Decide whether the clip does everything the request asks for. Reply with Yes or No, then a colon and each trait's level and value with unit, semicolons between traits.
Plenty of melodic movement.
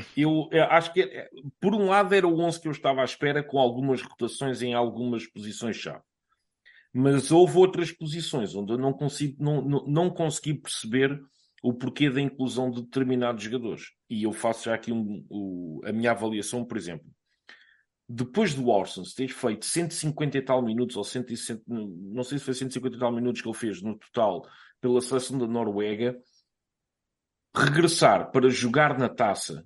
No: average, 3.7 semitones